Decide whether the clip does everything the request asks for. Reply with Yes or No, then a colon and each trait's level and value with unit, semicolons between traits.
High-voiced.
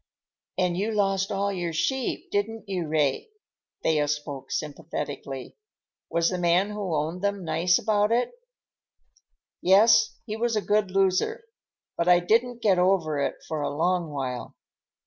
No: medium, 180 Hz